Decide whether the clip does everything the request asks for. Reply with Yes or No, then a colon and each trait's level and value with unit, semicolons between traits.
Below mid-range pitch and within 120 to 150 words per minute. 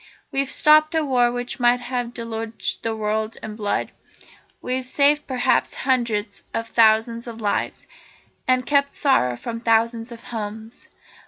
No: high, 235 Hz; average, 145 wpm